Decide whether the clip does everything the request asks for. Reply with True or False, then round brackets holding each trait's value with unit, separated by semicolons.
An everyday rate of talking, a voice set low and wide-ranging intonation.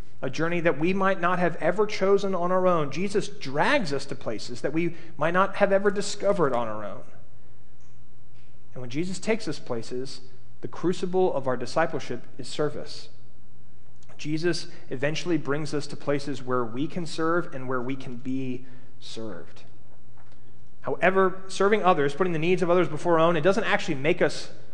False (175 wpm; 160 Hz; 6.1 semitones)